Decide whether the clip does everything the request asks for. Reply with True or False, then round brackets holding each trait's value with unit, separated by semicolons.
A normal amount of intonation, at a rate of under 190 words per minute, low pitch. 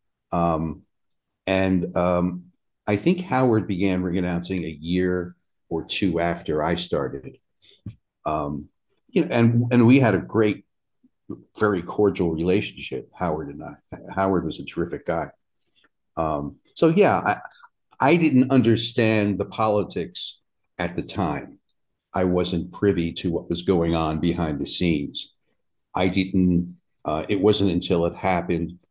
True (3.3 semitones; 140 wpm; 90 Hz)